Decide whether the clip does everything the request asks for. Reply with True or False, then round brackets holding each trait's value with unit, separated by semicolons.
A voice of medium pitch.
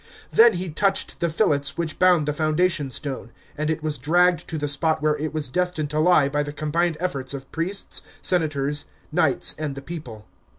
True (155 Hz)